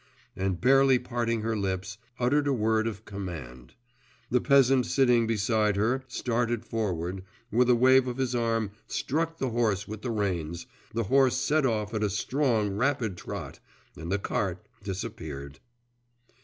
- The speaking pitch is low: Yes, low, 110 Hz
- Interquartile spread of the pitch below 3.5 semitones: No, average, 4.2 semitones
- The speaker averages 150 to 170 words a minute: Yes, average, 155 wpm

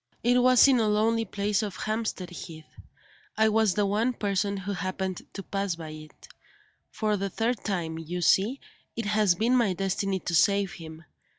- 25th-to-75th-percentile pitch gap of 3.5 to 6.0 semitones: No, average, 3.1 semitones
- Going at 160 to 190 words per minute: Yes, average, 180 wpm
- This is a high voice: Yes, high, 200 Hz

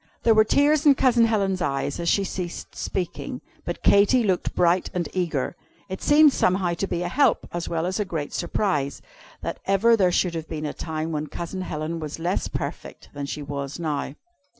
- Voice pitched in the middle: Yes, medium, 175 Hz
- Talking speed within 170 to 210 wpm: Yes, average, 195 wpm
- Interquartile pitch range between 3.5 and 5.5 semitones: Yes, average, 4.2 semitones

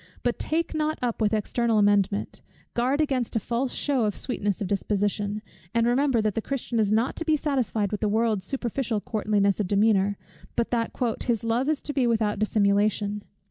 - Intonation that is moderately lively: Yes, average, 3.2 semitones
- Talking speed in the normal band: Yes, average, 185 wpm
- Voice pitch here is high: Yes, high, 225 Hz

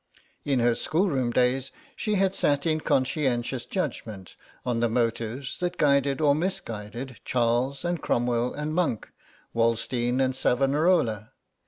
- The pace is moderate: No, slow, 130 wpm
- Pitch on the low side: Yes, low, 130 Hz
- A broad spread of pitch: No, average, 4.0 semitones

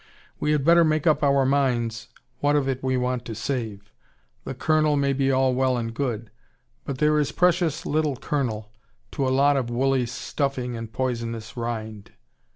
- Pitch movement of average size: Yes, average, 3.5 semitones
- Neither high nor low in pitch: No, low, 130 Hz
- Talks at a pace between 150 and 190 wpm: Yes, average, 175 wpm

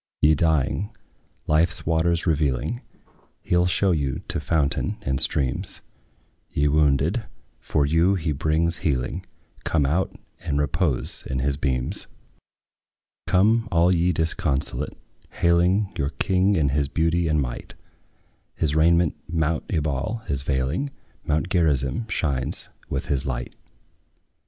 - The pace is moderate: No, slow, 125 wpm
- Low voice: Yes, very low, 80 Hz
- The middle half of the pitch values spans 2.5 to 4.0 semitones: Yes, average, 3.6 semitones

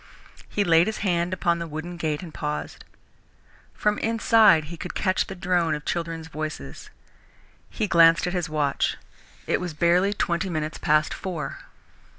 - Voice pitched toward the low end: No, medium, 170 Hz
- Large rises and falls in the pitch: No, average, 2.9 semitones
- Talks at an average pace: Yes, average, 160 wpm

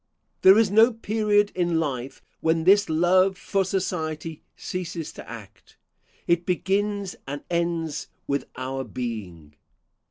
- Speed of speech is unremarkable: No, slow, 125 wpm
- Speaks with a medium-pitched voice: Yes, medium, 170 Hz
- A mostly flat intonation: No, average, 4.6 semitones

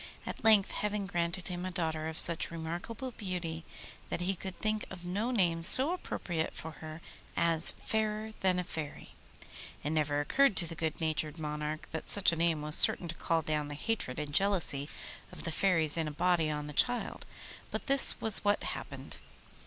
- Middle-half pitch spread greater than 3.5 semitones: Yes, average, 4.0 semitones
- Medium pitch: Yes, medium, 170 Hz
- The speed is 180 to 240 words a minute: Yes, average, 190 wpm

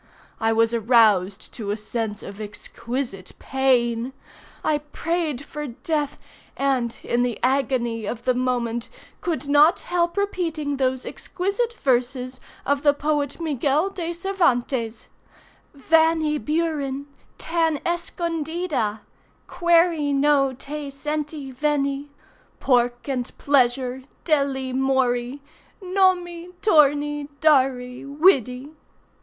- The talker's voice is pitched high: Yes, very high, 275 Hz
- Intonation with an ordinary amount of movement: Yes, average, 4.1 semitones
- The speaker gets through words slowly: Yes, slow, 105 wpm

